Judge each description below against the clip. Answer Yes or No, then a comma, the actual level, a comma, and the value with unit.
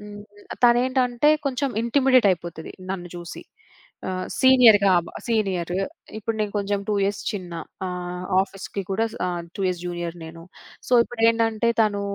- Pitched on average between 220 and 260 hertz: No, high, 205 Hz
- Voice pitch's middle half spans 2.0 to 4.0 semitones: No, average, 4.5 semitones